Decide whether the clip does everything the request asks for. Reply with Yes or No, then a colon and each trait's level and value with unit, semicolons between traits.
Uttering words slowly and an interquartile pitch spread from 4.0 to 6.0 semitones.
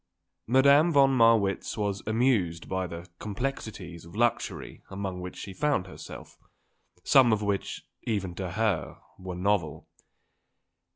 Yes: slow, 125 wpm; average, 4.4 semitones